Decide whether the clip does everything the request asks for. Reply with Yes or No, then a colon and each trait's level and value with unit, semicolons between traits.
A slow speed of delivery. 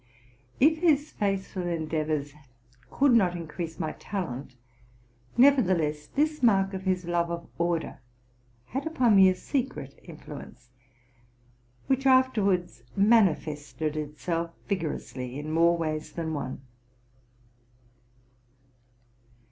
Yes: slow, 105 wpm